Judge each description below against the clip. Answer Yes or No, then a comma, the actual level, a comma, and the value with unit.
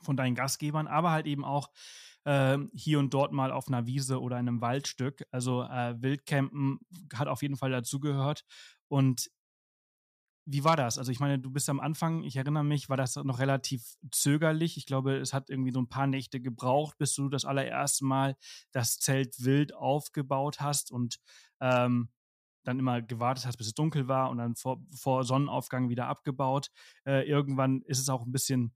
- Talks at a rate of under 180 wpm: No, average, 185 wpm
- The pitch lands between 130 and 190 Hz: Yes, low, 135 Hz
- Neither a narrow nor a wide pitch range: No, narrow, 2.0 semitones